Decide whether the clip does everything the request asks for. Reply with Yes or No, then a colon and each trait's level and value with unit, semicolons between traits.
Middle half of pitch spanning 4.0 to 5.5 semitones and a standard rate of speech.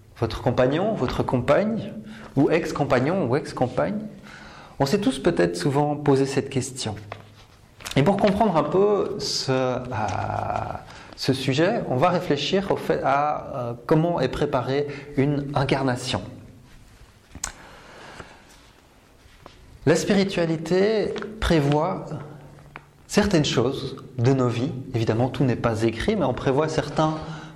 No: average, 4.9 semitones; slow, 120 wpm